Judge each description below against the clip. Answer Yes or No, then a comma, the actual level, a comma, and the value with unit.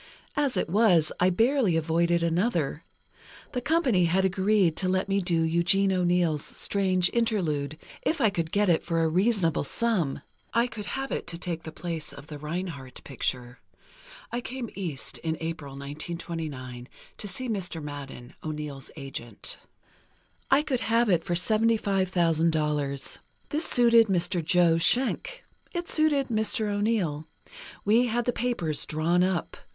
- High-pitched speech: No, medium, 180 Hz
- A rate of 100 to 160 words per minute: Yes, average, 145 wpm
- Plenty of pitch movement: Yes, wide, 5.7 semitones